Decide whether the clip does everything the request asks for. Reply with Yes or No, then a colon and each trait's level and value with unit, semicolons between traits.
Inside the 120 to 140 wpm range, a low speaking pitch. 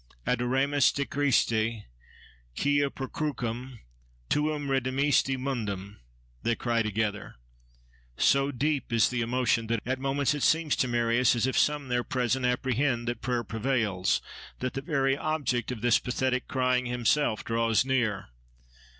Yes: slow, 135 wpm; low, 125 Hz